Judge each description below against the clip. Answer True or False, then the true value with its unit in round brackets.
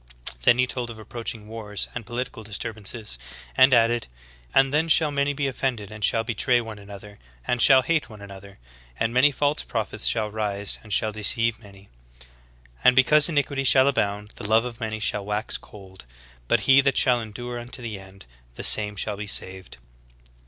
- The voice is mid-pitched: False (115 Hz)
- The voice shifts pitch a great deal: False (3.6 semitones)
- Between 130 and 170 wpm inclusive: False (190 wpm)